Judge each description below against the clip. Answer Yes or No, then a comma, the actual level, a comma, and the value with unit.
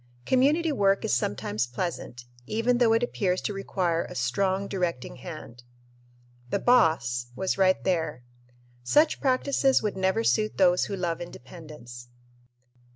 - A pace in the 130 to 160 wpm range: Yes, slow, 135 wpm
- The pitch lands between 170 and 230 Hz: Yes, medium, 185 Hz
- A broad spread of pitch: Yes, wide, 8.7 semitones